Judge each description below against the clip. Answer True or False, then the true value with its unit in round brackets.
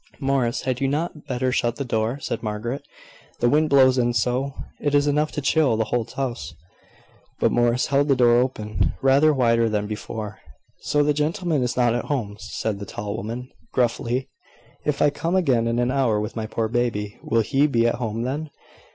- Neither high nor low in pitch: False (125 Hz)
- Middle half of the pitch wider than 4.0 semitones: False (3.4 semitones)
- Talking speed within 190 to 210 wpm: True (195 wpm)